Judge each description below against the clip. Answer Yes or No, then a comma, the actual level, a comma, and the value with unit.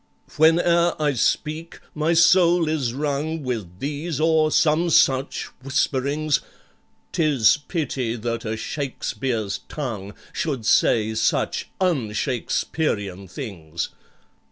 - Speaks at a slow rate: Yes, slow, 105 wpm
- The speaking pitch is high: No, medium, 140 Hz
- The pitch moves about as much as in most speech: No, wide, 5.9 semitones